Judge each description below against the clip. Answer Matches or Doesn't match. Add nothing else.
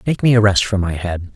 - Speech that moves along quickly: Matches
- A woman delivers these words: Doesn't match